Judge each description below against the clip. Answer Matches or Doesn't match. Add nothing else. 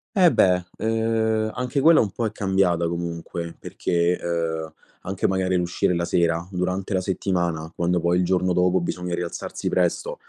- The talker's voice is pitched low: Matches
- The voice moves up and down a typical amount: Doesn't match